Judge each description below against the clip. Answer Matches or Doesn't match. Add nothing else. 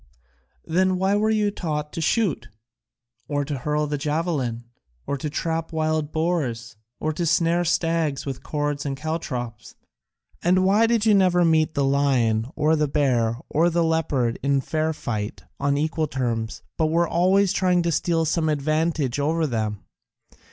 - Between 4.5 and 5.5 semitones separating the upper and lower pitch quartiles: Doesn't match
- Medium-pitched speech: Matches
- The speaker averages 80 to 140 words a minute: Doesn't match